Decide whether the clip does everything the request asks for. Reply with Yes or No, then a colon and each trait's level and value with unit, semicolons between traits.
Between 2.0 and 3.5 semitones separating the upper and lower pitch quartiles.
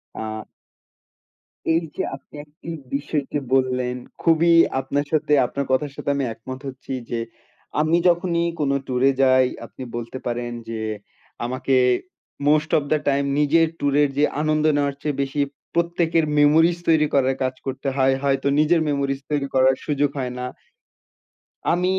Yes: average, 2.7 semitones